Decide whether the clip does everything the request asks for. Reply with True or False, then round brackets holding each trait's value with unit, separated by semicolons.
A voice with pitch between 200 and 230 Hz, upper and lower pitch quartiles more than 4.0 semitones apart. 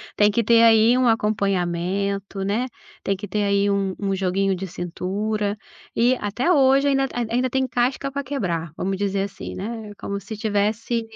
False (205 Hz; 3.2 semitones)